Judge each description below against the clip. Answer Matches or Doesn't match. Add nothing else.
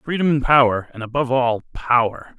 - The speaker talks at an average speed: Matches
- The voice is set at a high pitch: Doesn't match